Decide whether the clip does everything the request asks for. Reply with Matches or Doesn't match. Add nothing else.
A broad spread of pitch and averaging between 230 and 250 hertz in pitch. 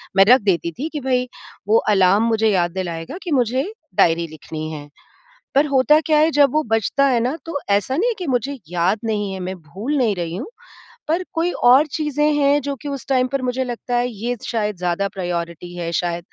Matches